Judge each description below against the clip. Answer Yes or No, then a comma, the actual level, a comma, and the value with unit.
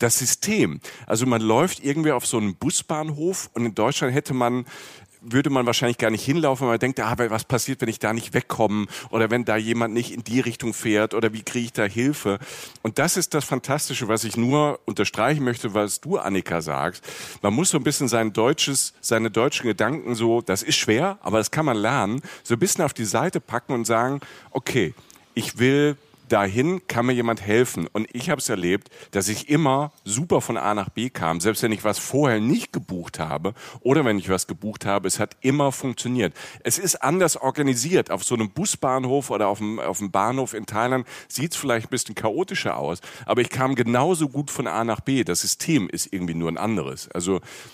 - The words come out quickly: Yes, fast, 215 wpm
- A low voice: Yes, low, 120 Hz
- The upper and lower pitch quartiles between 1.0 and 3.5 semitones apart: No, average, 4.1 semitones